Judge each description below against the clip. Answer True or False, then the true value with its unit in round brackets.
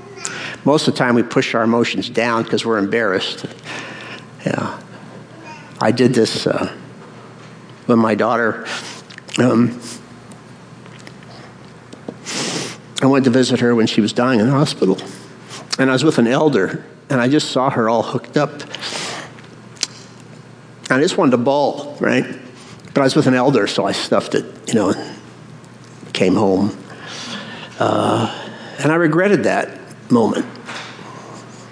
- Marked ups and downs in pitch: False (2.9 semitones)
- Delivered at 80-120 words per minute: False (140 wpm)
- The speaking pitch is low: True (125 Hz)